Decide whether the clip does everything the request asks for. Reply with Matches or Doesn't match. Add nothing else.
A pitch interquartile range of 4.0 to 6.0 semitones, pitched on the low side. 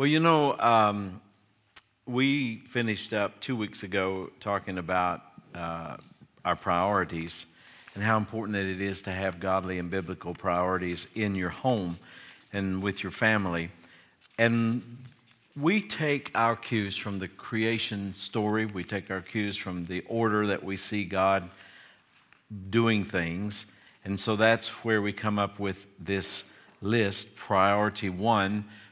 Doesn't match